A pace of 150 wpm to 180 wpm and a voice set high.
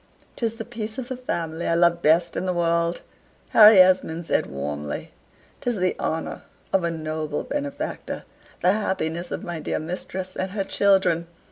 No: average, 165 wpm; medium, 175 Hz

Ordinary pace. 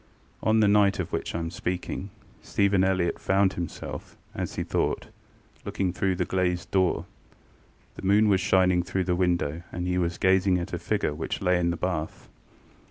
Yes: average, 180 wpm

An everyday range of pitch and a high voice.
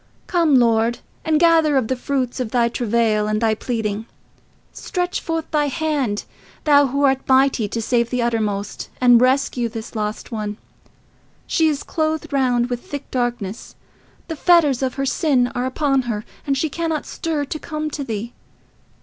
Yes: average, 4.3 semitones; very high, 255 Hz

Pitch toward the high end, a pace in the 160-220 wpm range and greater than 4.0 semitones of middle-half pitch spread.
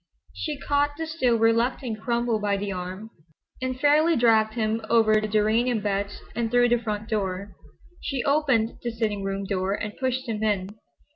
No: high, 225 Hz; average, 170 wpm; average, 3.0 semitones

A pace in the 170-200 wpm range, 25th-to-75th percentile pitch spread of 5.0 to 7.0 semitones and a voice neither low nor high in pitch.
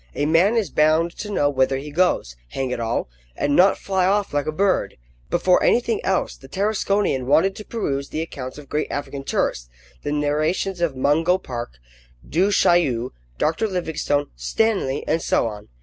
Yes: average, 175 wpm; wide, 5.5 semitones; medium, 155 Hz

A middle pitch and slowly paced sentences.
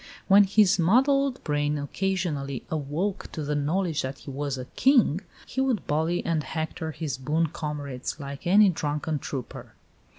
No: medium, 155 Hz; average, 155 wpm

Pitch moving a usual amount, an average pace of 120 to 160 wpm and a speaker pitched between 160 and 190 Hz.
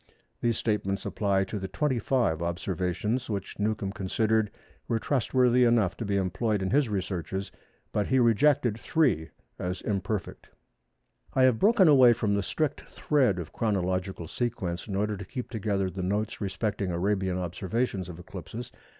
No: average, 4.1 semitones; average, 150 wpm; low, 105 Hz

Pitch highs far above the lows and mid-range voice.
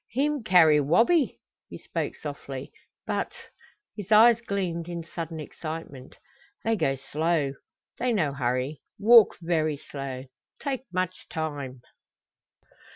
Yes: wide, 7.0 semitones; medium, 165 Hz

